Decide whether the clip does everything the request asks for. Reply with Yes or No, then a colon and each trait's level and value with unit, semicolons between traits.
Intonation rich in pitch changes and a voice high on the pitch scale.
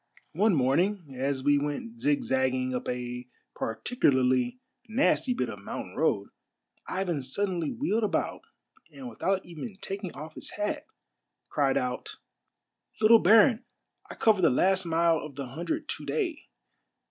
No: wide, 8.6 semitones; medium, 175 Hz